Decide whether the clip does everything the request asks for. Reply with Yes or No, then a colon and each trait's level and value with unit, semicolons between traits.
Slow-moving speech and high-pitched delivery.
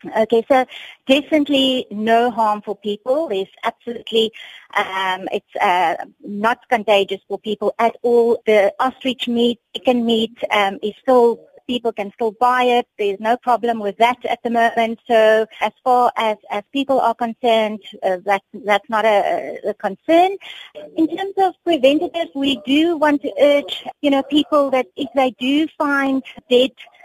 No: average, 165 wpm; high, 240 Hz